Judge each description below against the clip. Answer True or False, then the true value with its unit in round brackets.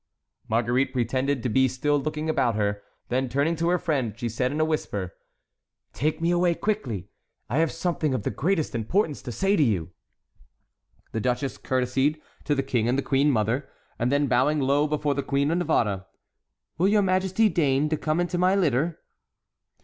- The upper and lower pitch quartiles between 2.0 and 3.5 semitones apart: False (4.6 semitones)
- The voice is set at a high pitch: False (140 Hz)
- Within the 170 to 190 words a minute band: True (180 wpm)